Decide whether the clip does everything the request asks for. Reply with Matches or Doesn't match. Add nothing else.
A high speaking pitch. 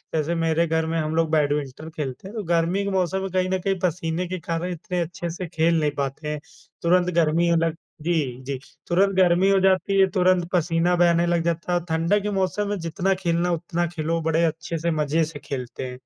Doesn't match